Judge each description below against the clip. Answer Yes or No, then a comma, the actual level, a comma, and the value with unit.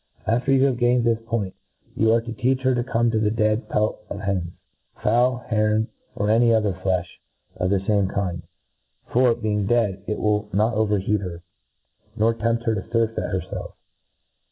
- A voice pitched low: Yes, low, 110 Hz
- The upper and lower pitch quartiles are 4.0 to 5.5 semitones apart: No, narrow, 2.4 semitones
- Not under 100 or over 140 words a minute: No, average, 180 wpm